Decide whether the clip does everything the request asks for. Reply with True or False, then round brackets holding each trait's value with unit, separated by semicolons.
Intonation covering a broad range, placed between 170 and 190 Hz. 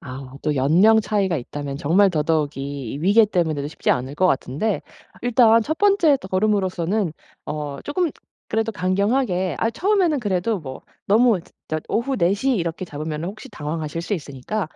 True (6.5 semitones; 185 Hz)